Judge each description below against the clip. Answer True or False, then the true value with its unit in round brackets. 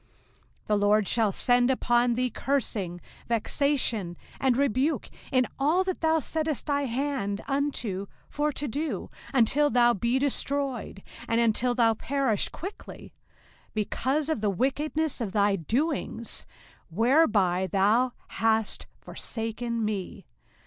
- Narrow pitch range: False (4.7 semitones)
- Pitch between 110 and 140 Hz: False (245 Hz)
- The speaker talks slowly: True (125 wpm)